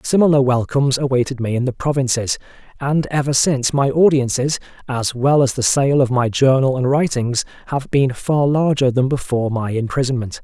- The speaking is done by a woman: No, male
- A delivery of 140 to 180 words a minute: Yes, average, 170 wpm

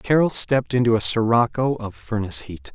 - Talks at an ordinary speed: Yes, average, 175 wpm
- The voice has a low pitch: Yes, low, 115 Hz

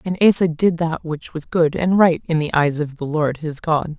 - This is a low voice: No, medium, 160 Hz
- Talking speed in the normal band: No, fast, 255 wpm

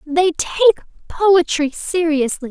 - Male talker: No, female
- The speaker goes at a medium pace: No, slow, 95 wpm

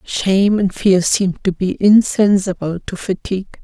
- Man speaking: No, female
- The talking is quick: No, average, 150 wpm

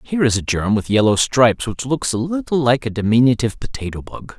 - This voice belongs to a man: Yes, male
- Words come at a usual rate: No, fast, 220 wpm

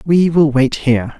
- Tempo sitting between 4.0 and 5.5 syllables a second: Yes, 4.7 syllables/s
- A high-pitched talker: No, medium, 145 Hz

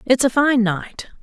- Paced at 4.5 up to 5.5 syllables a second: No, 4.1 syllables/s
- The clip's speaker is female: Yes, female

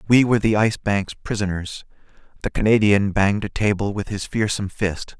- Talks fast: No, average, 175 wpm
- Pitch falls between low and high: No, low, 100 Hz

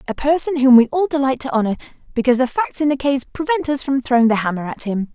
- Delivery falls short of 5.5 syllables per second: No, 6.5 syllables/s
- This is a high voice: Yes, very high, 265 Hz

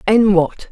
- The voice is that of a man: No, female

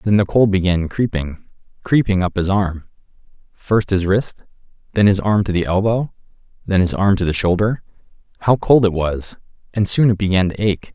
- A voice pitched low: Yes, low, 100 Hz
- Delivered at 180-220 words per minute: Yes, average, 185 wpm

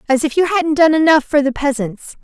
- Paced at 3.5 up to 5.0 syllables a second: No, 5.5 syllables/s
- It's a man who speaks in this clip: No, female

